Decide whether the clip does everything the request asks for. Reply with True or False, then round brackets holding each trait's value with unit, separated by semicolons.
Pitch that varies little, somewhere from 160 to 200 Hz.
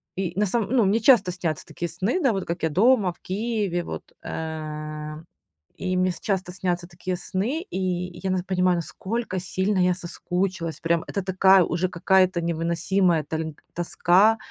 True (2.2 semitones; 185 Hz)